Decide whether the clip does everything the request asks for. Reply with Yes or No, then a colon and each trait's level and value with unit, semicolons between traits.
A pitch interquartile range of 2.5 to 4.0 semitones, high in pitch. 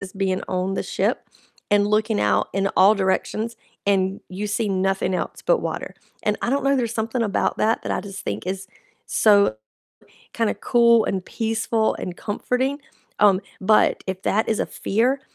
Yes: average, 2.9 semitones; high, 205 Hz